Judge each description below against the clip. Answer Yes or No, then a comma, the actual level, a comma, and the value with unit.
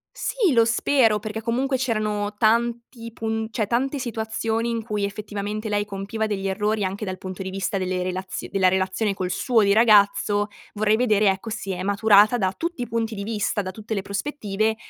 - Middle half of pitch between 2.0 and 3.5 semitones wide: Yes, narrow, 2.4 semitones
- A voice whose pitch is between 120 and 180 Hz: No, high, 215 Hz